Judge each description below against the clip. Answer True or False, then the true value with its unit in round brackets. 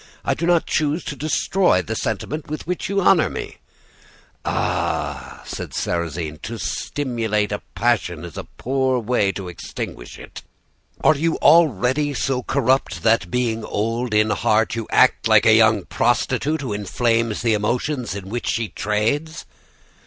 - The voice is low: True (120 Hz)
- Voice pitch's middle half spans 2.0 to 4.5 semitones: False (5.6 semitones)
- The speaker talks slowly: False (155 wpm)